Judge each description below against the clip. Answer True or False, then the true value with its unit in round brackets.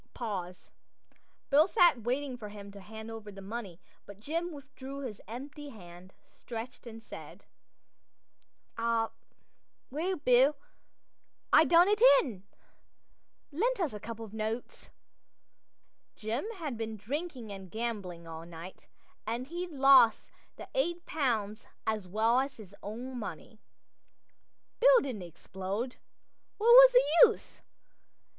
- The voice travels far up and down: True (5.7 semitones)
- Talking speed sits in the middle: False (125 wpm)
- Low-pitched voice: False (235 Hz)